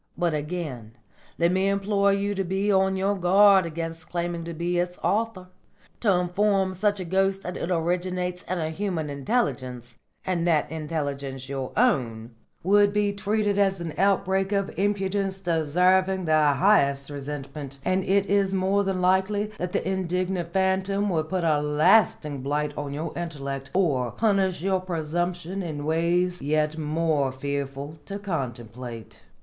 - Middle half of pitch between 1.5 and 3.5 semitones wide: No, average, 4.3 semitones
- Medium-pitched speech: Yes, medium, 175 Hz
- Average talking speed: Yes, average, 155 wpm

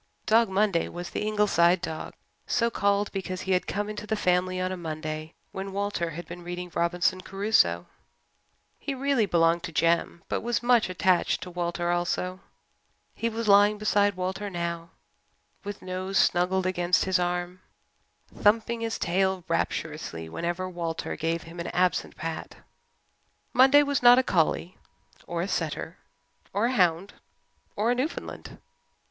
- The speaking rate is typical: Yes, average, 155 wpm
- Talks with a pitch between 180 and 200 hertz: Yes, medium, 185 Hz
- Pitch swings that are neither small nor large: Yes, average, 3.2 semitones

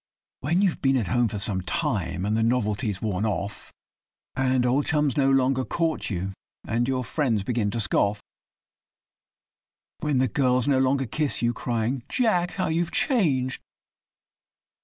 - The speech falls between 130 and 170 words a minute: Yes, average, 160 wpm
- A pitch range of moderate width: Yes, average, 4.5 semitones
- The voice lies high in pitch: No, low, 125 Hz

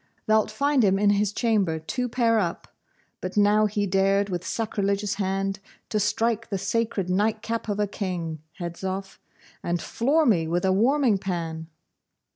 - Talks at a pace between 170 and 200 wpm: No, average, 160 wpm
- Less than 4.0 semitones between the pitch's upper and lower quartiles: Yes, average, 2.9 semitones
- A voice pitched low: No, high, 200 Hz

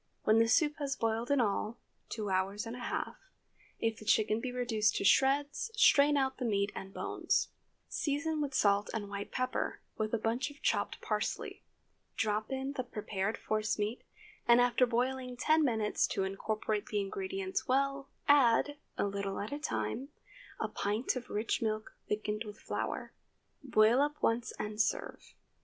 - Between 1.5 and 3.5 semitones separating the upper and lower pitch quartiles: No, average, 4.3 semitones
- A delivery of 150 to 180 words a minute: Yes, average, 170 wpm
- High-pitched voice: Yes, high, 230 Hz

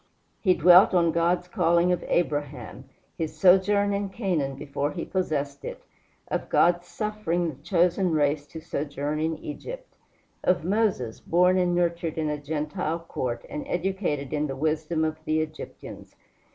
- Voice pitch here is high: No, medium, 165 Hz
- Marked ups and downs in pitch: No, average, 3.3 semitones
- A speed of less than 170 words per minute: Yes, average, 150 wpm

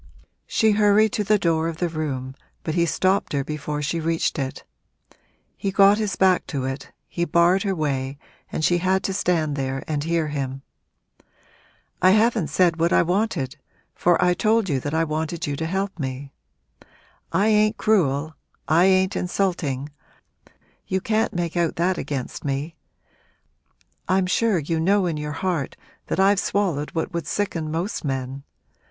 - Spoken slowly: No, average, 165 wpm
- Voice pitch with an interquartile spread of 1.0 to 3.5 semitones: No, average, 4.5 semitones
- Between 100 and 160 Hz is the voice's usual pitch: No, medium, 170 Hz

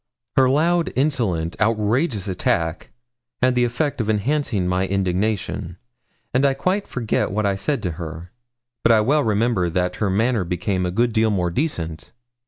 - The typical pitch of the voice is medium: No, low, 105 Hz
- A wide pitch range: Yes, wide, 5.7 semitones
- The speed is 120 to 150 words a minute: No, average, 165 wpm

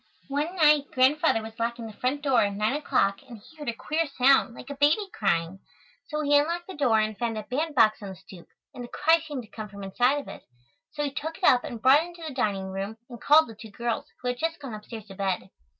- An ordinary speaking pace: No, fast, 255 wpm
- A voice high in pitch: Yes, very high, 250 Hz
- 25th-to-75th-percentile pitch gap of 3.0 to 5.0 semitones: No, wide, 5.5 semitones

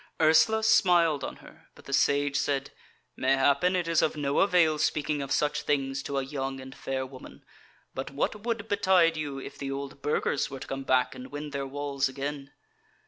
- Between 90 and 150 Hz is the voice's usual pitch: Yes, medium, 140 Hz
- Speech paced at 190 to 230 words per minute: Yes, average, 195 wpm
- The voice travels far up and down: No, average, 2.7 semitones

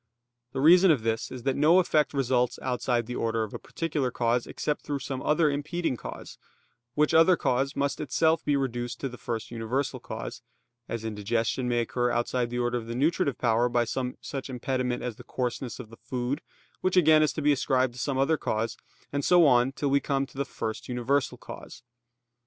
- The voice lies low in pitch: Yes, low, 130 Hz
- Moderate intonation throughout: Yes, average, 3.1 semitones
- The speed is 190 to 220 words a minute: Yes, fast, 205 wpm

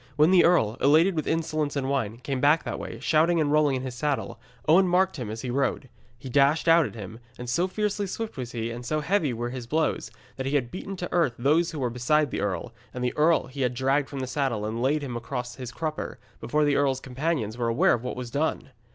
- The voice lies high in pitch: No, medium, 140 Hz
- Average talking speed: No, fast, 250 wpm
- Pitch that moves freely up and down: No, average, 4.2 semitones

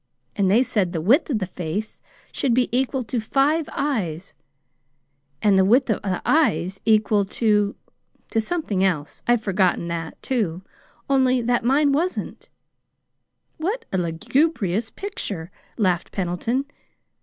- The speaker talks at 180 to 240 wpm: No, slow, 135 wpm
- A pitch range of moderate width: No, wide, 6.0 semitones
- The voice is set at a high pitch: Yes, high, 215 Hz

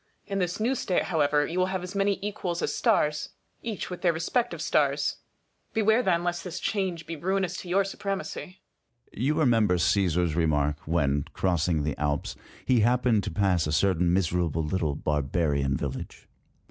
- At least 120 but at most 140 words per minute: No, average, 170 wpm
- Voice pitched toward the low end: Yes, low, 130 Hz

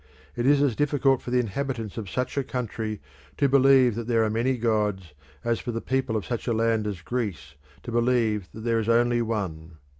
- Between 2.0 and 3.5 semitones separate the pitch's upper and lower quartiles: Yes, average, 2.8 semitones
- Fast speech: Yes, fast, 210 wpm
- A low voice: Yes, low, 115 Hz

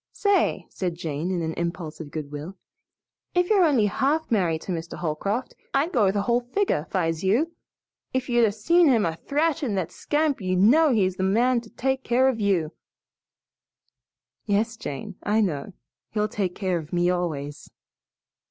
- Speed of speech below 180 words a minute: Yes, average, 170 wpm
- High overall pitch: Yes, high, 205 Hz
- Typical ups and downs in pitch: No, wide, 6.9 semitones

